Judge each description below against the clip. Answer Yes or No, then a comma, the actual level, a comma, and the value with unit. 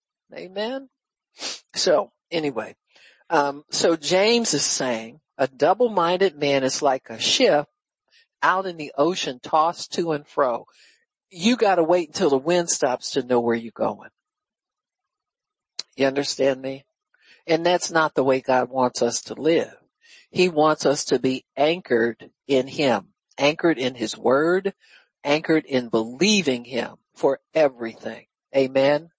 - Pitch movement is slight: No, average, 5.3 semitones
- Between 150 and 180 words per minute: No, average, 140 wpm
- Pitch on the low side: No, medium, 145 Hz